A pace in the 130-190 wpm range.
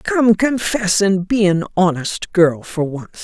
Yes: average, 165 wpm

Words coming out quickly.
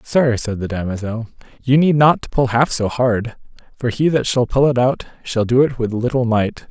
Yes: fast, 225 wpm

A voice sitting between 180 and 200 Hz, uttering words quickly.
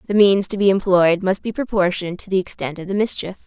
Yes: high, 190 Hz; fast, 245 wpm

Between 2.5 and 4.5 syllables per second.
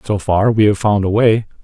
No: 5.0 syllables/s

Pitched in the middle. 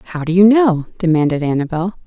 Yes: medium, 175 Hz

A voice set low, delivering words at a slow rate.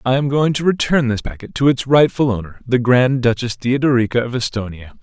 No: low, 125 Hz; fast, 205 wpm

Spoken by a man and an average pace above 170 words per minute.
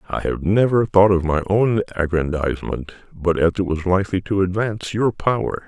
Yes: male; average, 180 wpm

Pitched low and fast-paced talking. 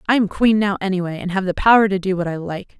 No: high, 195 Hz; fast, 300 wpm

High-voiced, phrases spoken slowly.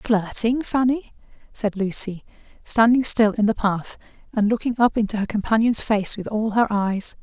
No: high, 215 Hz; average, 165 wpm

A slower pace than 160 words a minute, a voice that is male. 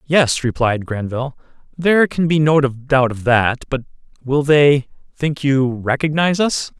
Yes: average, 150 wpm; male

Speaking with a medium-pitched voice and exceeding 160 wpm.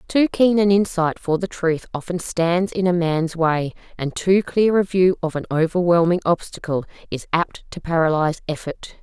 Yes: medium, 175 Hz; average, 180 wpm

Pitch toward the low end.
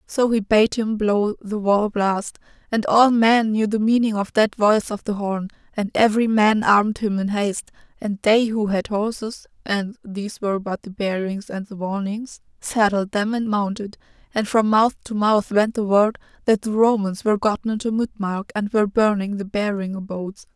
No: high, 210 Hz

